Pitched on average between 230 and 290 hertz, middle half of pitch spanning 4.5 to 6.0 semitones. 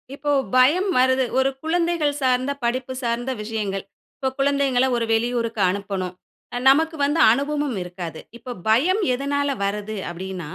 Yes: very high, 255 Hz; average, 5.0 semitones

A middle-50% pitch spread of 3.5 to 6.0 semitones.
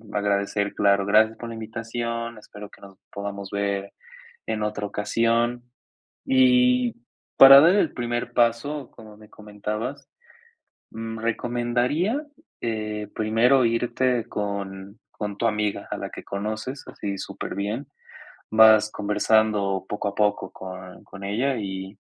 No: average, 2.7 semitones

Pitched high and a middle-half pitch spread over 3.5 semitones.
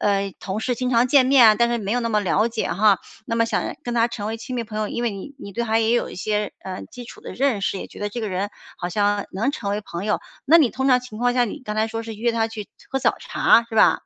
No: high, 225 Hz; average, 2.7 semitones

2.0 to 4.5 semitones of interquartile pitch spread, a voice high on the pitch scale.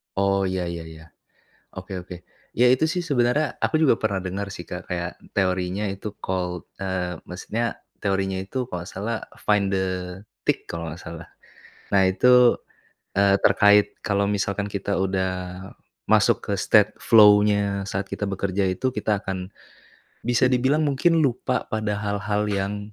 No: narrow, 2.5 semitones; low, 100 Hz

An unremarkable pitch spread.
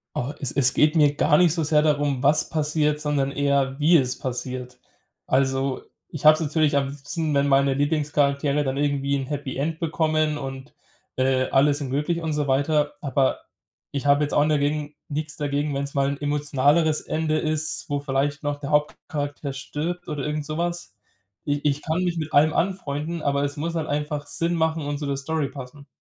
No: narrow, 1.8 semitones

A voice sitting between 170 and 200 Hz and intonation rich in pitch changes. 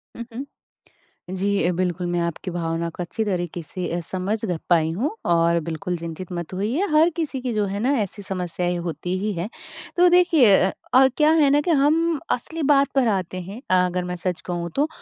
Yes: medium, 185 Hz; wide, 6.6 semitones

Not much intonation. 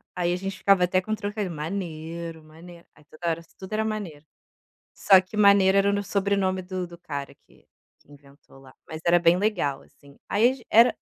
No: average, 3.6 semitones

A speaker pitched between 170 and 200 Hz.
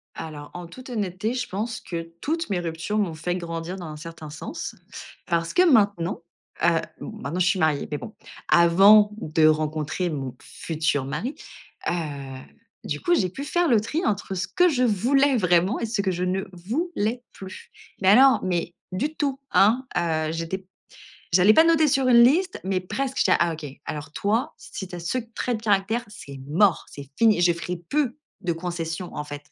Yes: medium, 185 Hz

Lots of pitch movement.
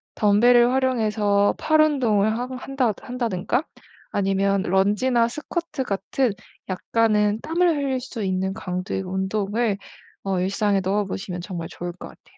No: average, 4.5 semitones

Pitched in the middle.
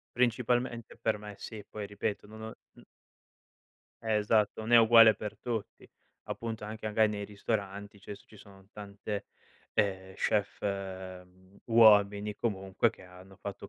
No: low, 105 Hz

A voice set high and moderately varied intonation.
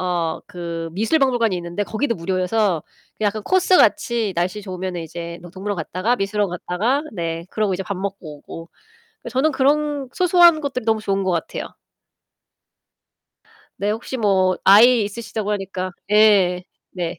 Yes: high, 200 Hz; average, 4.5 semitones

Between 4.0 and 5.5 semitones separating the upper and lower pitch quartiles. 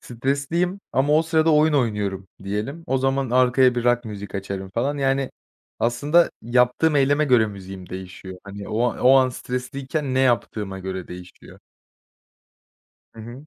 Yes: average, 5.2 semitones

